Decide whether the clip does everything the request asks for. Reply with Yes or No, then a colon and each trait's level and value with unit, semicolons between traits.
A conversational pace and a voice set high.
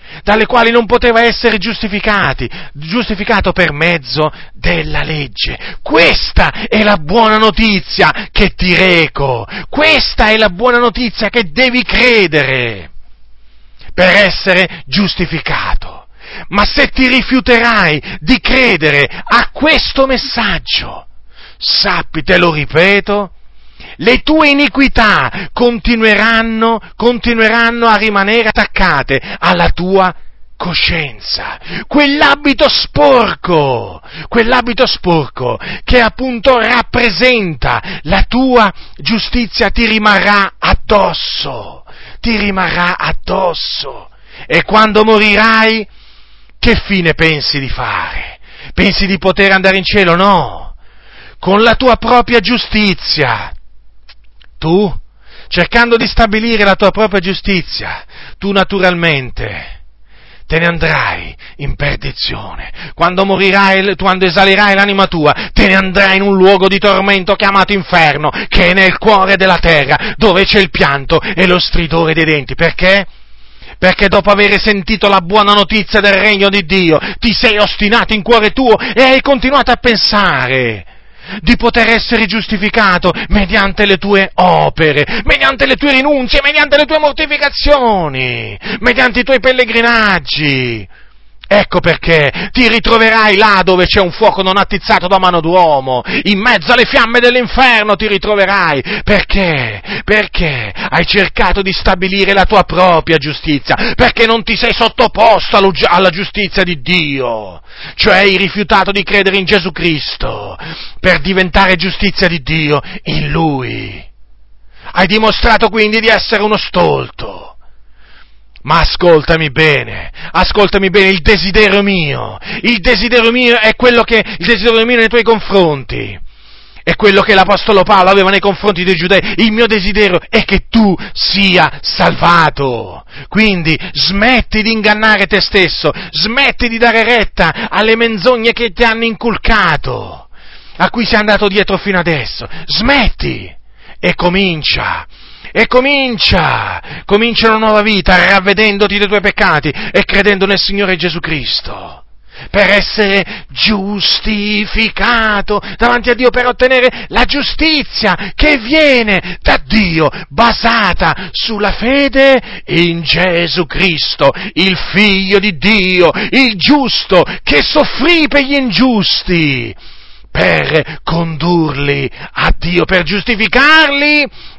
Yes: average, 125 wpm; high, 200 Hz